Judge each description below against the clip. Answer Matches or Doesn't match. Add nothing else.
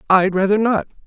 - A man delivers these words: Matches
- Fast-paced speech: Doesn't match